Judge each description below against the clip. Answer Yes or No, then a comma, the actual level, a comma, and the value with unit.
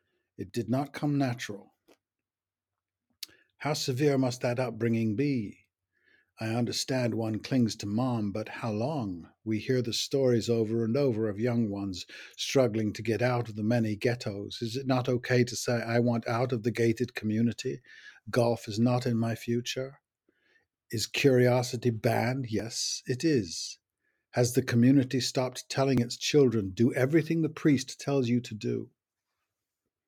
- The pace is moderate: Yes, average, 155 wpm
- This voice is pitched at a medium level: No, low, 120 Hz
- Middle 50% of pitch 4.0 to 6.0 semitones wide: No, narrow, 2.5 semitones